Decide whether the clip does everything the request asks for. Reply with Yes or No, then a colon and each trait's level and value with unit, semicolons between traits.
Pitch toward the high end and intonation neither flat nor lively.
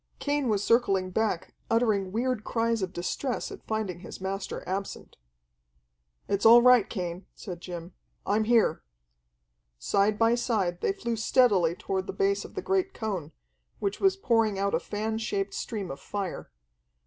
Yes: high, 210 Hz; average, 3.7 semitones